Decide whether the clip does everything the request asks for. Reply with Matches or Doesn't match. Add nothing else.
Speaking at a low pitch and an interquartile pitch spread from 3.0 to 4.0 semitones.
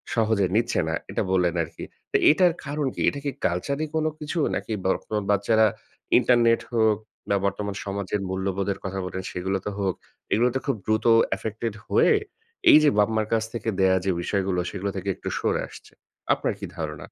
Matches